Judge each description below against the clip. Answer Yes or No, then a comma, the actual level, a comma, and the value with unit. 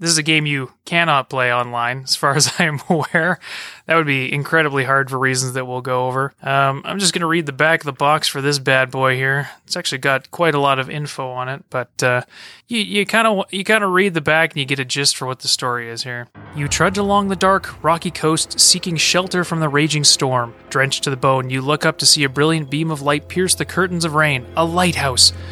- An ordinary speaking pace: No, fast, 250 wpm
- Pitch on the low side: No, medium, 145 Hz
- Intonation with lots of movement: No, average, 3.9 semitones